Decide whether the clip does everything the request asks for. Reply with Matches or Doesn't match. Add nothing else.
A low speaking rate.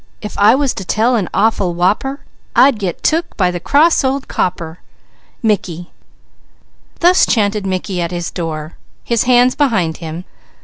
Doesn't match